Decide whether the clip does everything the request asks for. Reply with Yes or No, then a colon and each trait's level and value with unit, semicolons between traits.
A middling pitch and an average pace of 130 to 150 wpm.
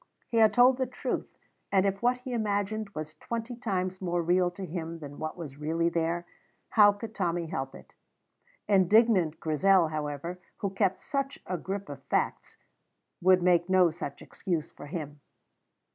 No: medium, 180 Hz; average, 165 wpm